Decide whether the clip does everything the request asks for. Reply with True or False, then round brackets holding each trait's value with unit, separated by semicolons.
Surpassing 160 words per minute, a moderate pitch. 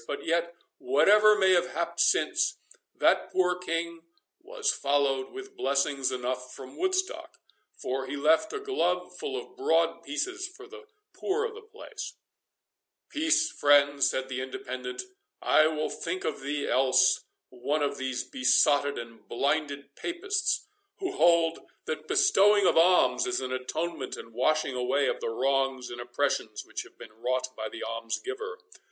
False (150 wpm; 155 Hz)